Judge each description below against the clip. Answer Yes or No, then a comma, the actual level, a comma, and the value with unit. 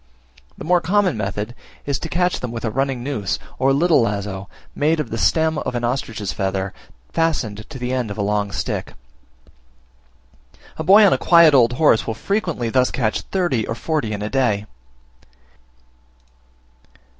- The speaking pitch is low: Yes, low, 125 Hz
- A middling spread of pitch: No, wide, 6.8 semitones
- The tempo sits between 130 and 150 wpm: No, average, 165 wpm